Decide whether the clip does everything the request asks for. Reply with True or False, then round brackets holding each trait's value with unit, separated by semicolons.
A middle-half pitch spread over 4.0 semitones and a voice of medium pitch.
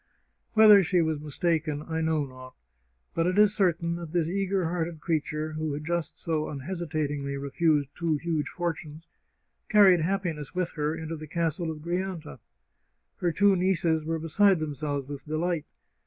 False (2.5 semitones; 160 Hz)